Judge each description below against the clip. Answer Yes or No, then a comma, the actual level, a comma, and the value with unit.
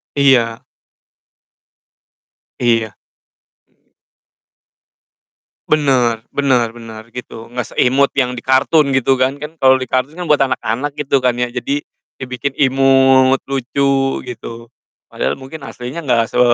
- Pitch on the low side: Yes, low, 130 Hz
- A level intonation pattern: Yes, narrow, 2.2 semitones